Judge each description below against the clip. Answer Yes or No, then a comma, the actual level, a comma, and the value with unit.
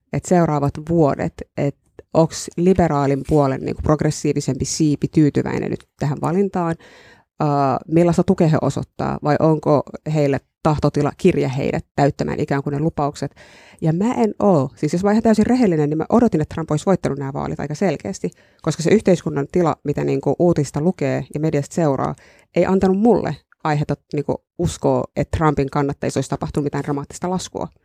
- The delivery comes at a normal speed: No, fast, 165 wpm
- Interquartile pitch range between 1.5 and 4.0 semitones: Yes, average, 3.5 semitones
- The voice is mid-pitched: Yes, medium, 150 Hz